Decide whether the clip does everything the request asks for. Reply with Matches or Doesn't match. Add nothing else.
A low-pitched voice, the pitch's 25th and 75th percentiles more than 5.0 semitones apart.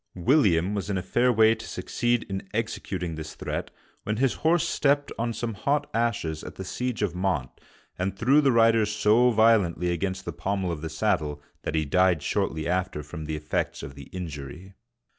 Matches